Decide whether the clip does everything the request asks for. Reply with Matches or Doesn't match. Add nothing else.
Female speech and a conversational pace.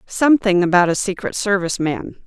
Matches